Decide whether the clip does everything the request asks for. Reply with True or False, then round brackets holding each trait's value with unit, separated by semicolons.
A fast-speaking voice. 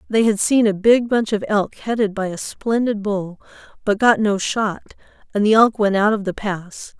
True (215 wpm)